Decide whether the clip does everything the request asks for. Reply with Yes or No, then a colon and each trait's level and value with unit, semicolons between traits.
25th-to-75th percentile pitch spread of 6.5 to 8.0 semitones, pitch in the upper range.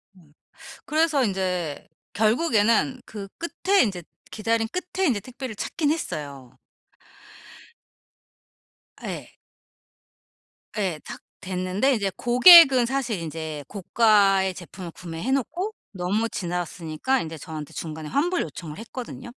Yes: wide, 6.9 semitones; high, 205 Hz